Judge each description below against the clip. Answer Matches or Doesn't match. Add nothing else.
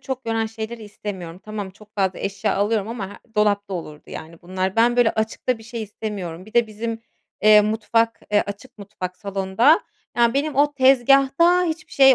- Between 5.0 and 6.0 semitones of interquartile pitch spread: Doesn't match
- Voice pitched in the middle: Doesn't match